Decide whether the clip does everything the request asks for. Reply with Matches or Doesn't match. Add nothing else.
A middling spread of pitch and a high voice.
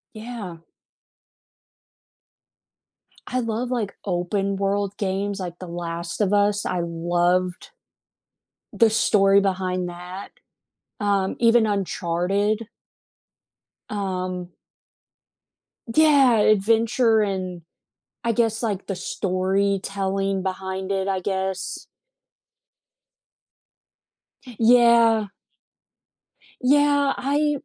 Matches